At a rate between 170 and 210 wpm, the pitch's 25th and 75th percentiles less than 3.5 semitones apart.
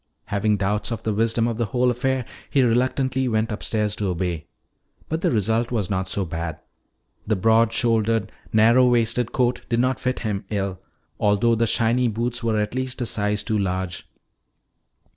Yes: average, 175 wpm; average, 2.9 semitones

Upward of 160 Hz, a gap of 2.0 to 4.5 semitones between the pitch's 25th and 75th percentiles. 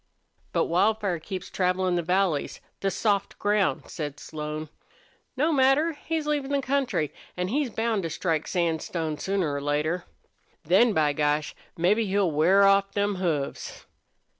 No: medium, 185 Hz; average, 5.1 semitones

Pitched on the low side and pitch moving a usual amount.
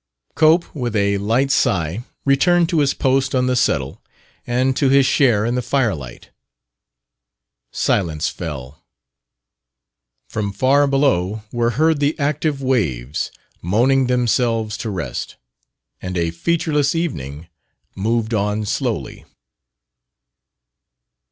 No: low, 120 Hz; wide, 5.8 semitones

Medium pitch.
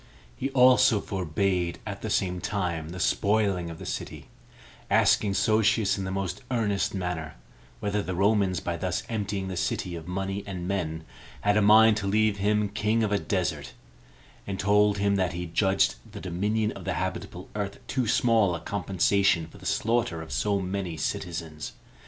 No: low, 100 Hz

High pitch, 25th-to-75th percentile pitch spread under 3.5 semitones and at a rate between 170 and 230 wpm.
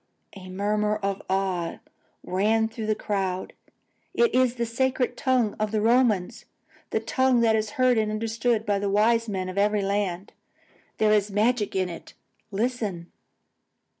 No: high, 215 Hz; average, 2.8 semitones; average, 160 wpm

